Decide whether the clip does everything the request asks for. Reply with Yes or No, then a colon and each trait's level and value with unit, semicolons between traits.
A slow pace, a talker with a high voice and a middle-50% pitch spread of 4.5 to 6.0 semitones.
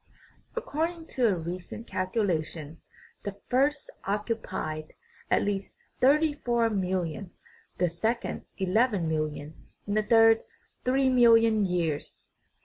Yes: slow, 115 wpm; high, 205 Hz; wide, 5.5 semitones